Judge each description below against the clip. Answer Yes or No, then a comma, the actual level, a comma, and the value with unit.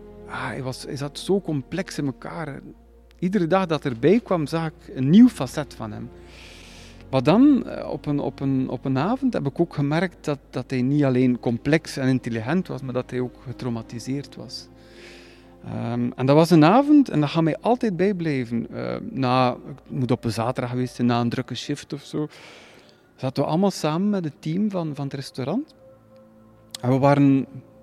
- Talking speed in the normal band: Yes, average, 190 wpm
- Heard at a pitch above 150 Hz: No, low, 135 Hz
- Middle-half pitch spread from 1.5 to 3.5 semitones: No, average, 4.7 semitones